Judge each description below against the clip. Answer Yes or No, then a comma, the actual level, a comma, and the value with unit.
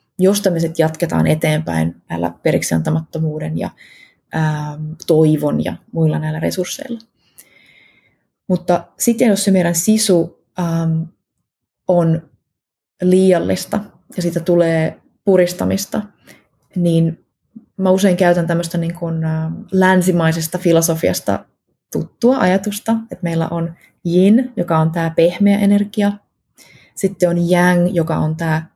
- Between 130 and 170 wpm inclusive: No, average, 105 wpm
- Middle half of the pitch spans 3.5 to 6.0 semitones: No, average, 2.7 semitones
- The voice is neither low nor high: Yes, medium, 170 Hz